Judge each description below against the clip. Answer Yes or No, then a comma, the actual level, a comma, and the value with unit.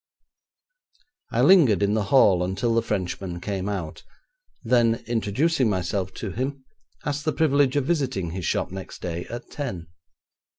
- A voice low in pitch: Yes, low, 110 Hz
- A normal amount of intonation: No, wide, 6.1 semitones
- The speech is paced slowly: No, average, 145 wpm